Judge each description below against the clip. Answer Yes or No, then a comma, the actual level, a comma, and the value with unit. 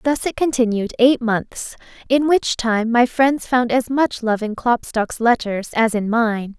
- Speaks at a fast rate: No, average, 180 wpm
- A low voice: No, high, 240 Hz